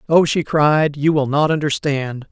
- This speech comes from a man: Yes, male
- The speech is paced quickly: No, average, 180 wpm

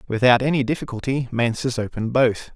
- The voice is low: Yes, low, 125 Hz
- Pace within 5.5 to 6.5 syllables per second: Yes, 6.0 syllables/s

